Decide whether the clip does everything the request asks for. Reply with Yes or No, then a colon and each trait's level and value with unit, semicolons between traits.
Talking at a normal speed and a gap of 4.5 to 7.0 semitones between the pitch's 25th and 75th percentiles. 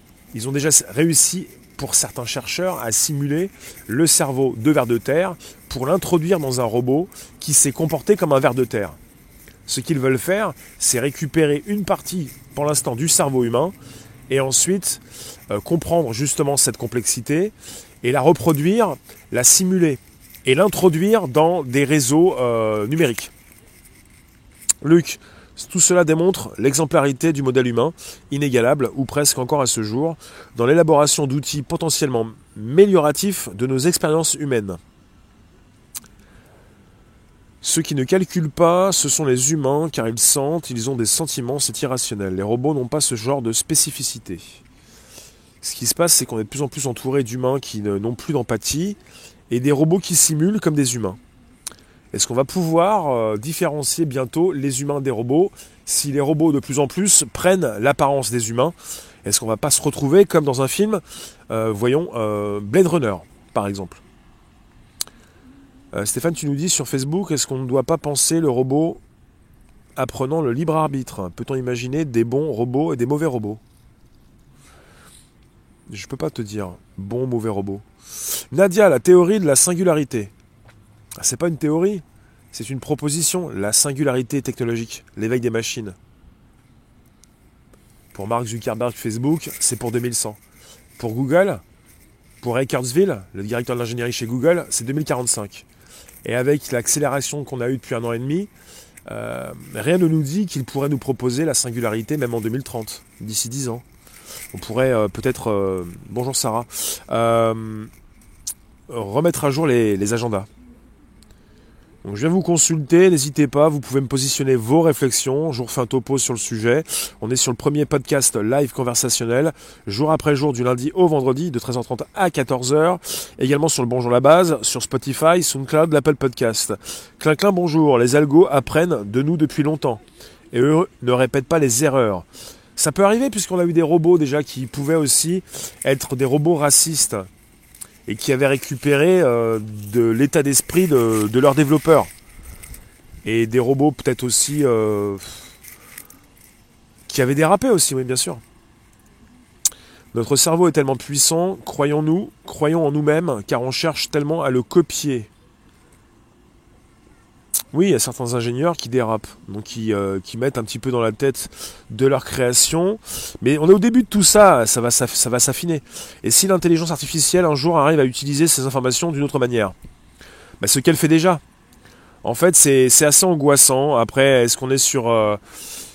Yes: average, 165 wpm; average, 5.1 semitones